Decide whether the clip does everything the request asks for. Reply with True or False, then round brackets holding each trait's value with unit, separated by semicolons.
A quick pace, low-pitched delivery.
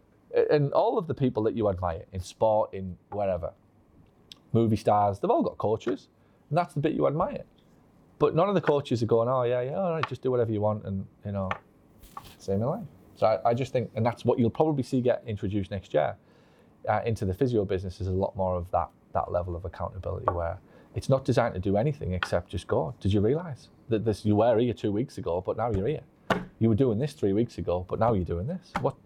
True (230 wpm; 110 Hz)